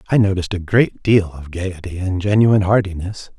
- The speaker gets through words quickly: No, average, 175 wpm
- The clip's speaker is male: Yes, male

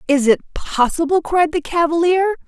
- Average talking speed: Yes, average, 145 wpm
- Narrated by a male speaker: No, female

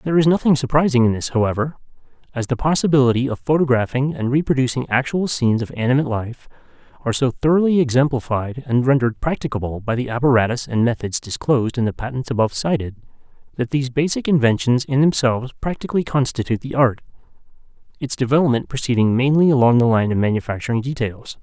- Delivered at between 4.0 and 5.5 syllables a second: No, 6.6 syllables/s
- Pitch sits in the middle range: No, low, 130 Hz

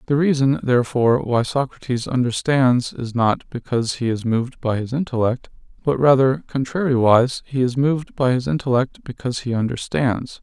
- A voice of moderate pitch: No, low, 125 Hz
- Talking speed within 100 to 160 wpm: Yes, average, 155 wpm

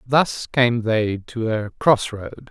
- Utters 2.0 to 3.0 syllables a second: Yes, 2.9 syllables/s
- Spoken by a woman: No, male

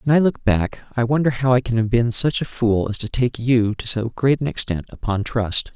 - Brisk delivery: Yes, fast, 260 wpm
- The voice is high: No, low, 120 Hz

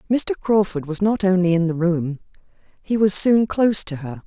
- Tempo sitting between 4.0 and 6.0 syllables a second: Yes, 5.1 syllables/s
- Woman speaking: Yes, female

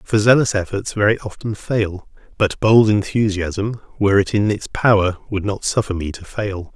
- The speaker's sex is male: Yes, male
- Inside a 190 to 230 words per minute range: No, average, 180 wpm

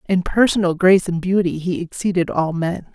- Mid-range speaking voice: Yes, medium, 180 Hz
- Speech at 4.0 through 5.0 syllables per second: No, 5.5 syllables/s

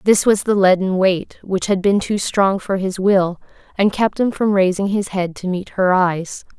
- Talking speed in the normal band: No, fast, 220 wpm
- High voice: Yes, high, 195 Hz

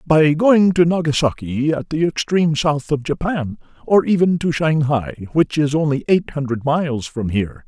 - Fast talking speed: No, average, 170 wpm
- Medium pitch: Yes, medium, 150 Hz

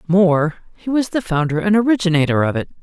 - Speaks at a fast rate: No, average, 190 wpm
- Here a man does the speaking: No, female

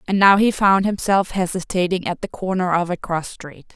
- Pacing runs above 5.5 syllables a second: No, 5.0 syllables/s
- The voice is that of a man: No, female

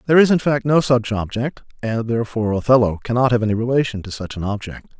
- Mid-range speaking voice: No, low, 120 Hz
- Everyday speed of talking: No, fast, 215 wpm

